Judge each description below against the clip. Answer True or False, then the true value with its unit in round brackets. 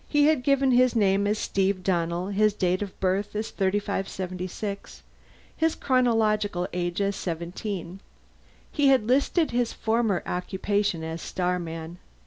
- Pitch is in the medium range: False (200 Hz)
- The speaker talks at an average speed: False (130 wpm)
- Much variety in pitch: False (3.8 semitones)